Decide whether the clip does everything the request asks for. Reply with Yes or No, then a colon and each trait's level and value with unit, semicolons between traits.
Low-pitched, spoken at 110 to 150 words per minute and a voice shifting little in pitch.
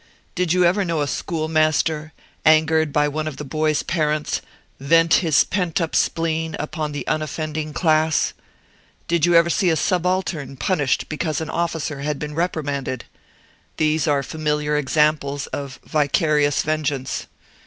No: medium, 155 Hz; average, 145 wpm; narrow, 1.8 semitones